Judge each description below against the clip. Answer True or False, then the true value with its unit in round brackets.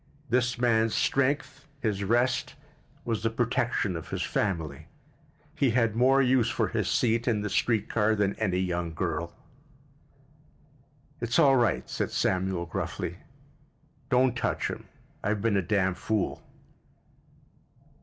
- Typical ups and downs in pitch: True (4.2 semitones)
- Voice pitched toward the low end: True (110 Hz)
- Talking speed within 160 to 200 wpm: False (135 wpm)